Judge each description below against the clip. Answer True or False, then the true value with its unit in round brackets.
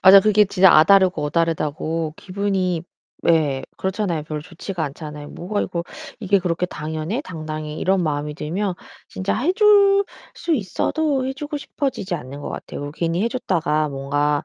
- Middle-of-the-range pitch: True (175 Hz)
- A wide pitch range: False (4.8 semitones)